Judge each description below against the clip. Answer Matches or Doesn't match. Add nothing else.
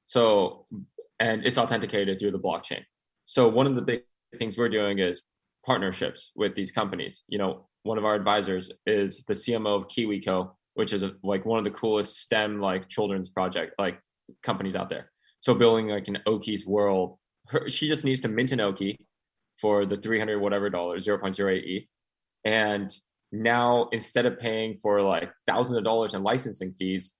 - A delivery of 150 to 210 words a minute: Matches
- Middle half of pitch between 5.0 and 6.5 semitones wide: Doesn't match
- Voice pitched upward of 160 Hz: Doesn't match